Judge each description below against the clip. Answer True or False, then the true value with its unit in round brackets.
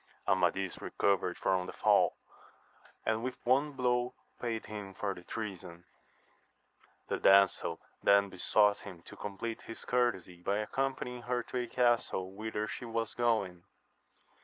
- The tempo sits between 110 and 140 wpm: True (135 wpm)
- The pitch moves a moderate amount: True (3.9 semitones)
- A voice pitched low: True (105 Hz)